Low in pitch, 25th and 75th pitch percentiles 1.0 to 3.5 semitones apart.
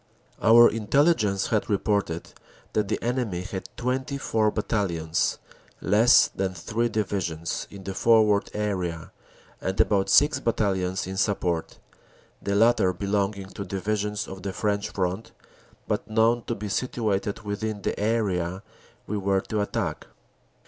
Yes: low, 100 Hz; narrow, 2.6 semitones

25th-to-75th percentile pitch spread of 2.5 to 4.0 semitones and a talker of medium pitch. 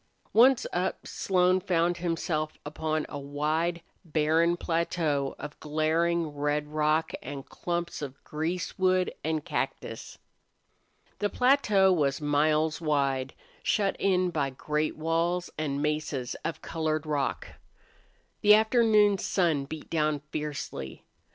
Yes: average, 2.9 semitones; medium, 160 Hz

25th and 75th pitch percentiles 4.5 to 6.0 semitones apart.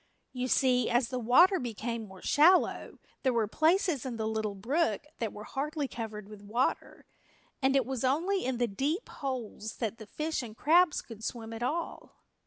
Yes: average, 4.8 semitones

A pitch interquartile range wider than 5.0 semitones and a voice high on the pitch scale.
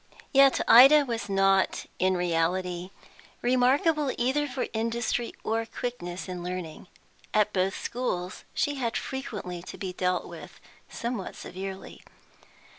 Yes: wide, 5.4 semitones; high, 210 Hz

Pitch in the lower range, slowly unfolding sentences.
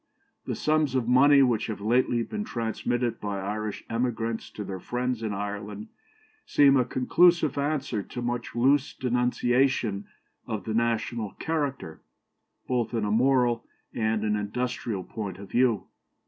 No: low, 120 Hz; average, 145 wpm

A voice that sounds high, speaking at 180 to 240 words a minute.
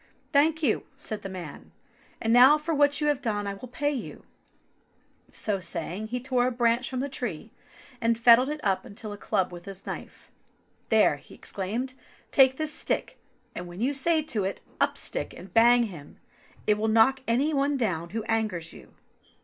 Yes: high, 230 Hz; average, 190 wpm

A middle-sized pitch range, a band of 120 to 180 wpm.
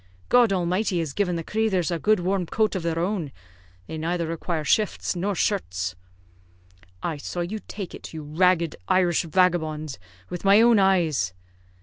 Yes: average, 3.4 semitones; average, 160 wpm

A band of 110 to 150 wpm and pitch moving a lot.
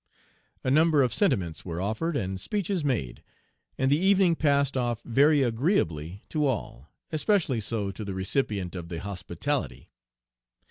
Yes: average, 145 wpm; wide, 8.0 semitones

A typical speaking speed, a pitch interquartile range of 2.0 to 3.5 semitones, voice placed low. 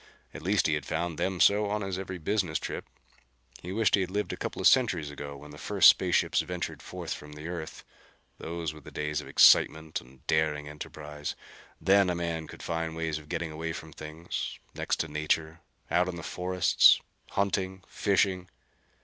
Yes: average, 190 wpm; average, 3.2 semitones; very low, 80 Hz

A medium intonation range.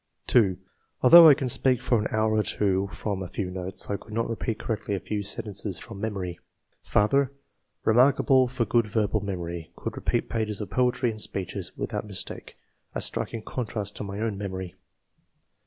Yes: average, 3.1 semitones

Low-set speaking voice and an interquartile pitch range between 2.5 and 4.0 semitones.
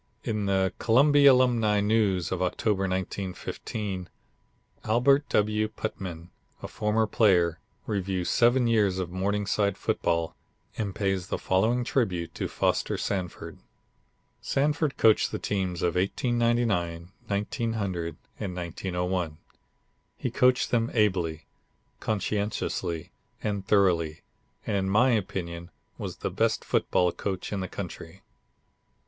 Yes: low, 100 Hz; average, 3.6 semitones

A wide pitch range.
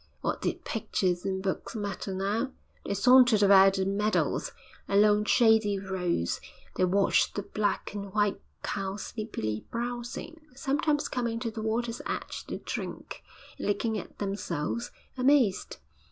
No: average, 3.2 semitones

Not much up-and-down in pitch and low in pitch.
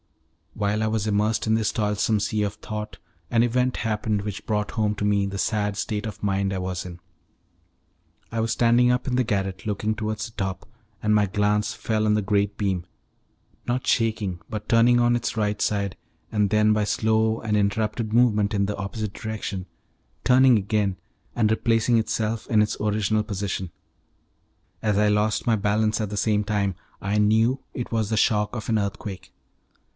Yes: narrow, 1.5 semitones; low, 105 Hz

